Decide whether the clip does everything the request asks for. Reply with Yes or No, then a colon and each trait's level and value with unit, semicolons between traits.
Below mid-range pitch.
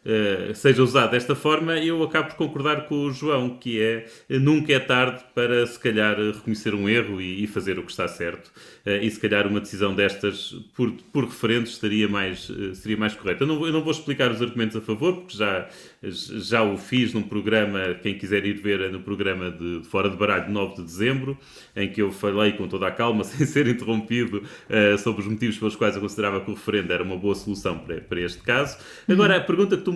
Yes: low, 110 Hz